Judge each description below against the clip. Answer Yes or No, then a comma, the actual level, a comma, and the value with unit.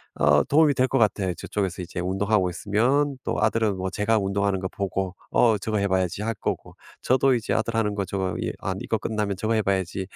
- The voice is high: No, low, 100 Hz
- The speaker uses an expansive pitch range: No, average, 2.9 semitones